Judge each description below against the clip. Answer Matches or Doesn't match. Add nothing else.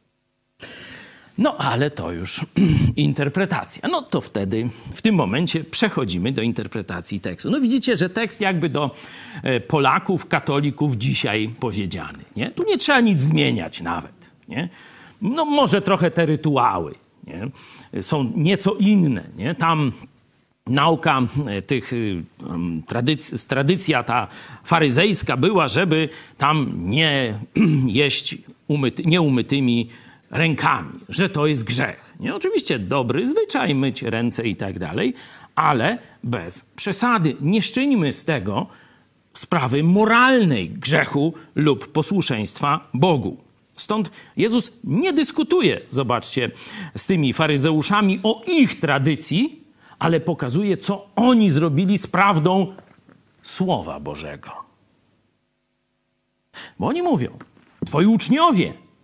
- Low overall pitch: Doesn't match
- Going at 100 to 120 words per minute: Matches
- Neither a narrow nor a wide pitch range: Doesn't match